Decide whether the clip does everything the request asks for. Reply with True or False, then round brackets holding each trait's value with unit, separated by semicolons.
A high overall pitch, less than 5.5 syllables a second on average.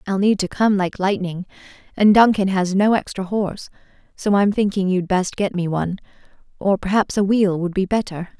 True (195 Hz; 5.3 syllables/s)